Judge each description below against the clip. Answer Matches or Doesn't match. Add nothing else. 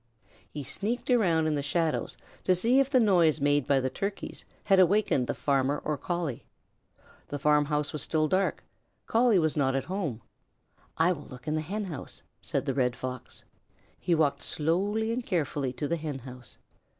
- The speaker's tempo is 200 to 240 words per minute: Doesn't match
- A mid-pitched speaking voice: Matches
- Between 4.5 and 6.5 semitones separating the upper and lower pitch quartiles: Matches